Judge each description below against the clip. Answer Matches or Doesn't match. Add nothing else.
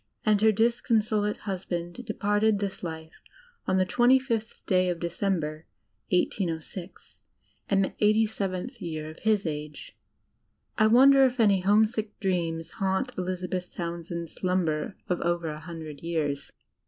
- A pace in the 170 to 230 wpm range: Doesn't match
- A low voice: Doesn't match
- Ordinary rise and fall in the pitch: Matches